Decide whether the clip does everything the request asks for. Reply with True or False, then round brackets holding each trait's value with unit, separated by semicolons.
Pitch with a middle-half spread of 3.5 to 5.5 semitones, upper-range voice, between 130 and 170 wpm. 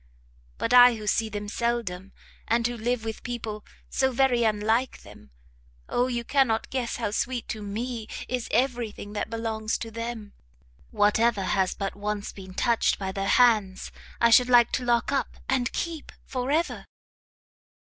False (2.8 semitones; 230 Hz; 165 wpm)